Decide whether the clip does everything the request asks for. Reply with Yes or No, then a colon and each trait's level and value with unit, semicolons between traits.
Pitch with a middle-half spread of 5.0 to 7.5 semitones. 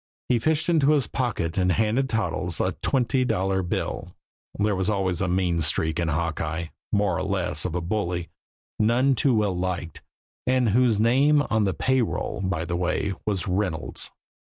Yes: wide, 5.5 semitones